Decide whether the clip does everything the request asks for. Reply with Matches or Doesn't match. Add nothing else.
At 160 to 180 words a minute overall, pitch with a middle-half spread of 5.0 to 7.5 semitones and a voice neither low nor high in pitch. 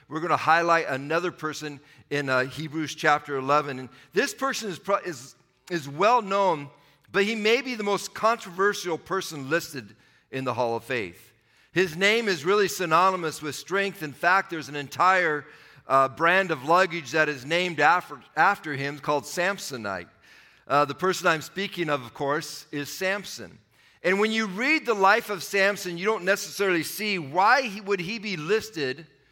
Matches